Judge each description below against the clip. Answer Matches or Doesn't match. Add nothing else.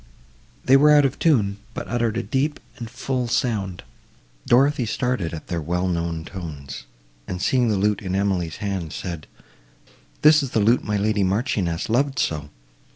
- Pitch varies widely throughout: Matches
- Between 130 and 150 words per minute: Doesn't match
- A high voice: Doesn't match